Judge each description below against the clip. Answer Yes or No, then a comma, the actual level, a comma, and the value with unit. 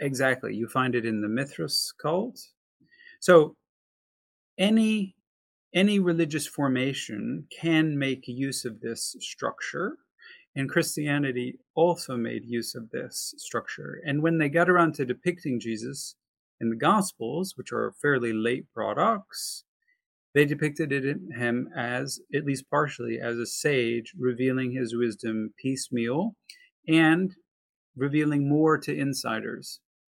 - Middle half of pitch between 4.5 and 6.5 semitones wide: Yes, average, 5.0 semitones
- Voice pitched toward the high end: No, medium, 140 Hz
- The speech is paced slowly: Yes, slow, 130 wpm